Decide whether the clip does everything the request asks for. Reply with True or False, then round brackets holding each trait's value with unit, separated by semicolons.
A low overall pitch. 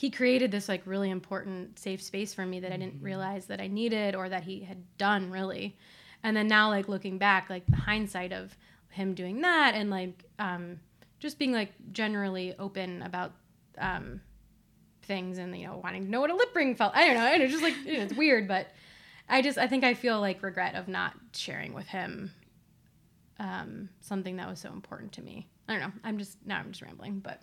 False (195 Hz)